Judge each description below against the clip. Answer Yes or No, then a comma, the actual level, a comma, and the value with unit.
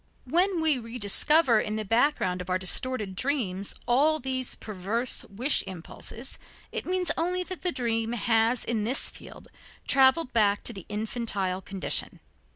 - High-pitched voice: Yes, high, 235 Hz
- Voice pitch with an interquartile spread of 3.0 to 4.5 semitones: No, average, 5.2 semitones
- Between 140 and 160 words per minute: Yes, average, 150 wpm